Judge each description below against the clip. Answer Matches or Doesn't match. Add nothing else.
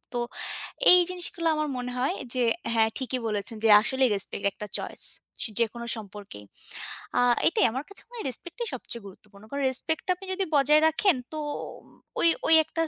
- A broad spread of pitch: Matches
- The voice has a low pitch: Doesn't match